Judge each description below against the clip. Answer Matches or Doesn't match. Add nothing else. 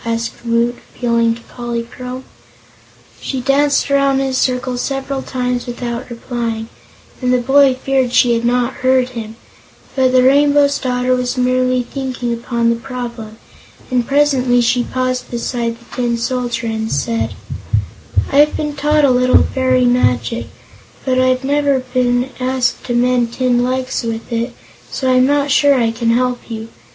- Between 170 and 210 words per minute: Doesn't match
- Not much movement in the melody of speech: Matches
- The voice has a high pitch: Matches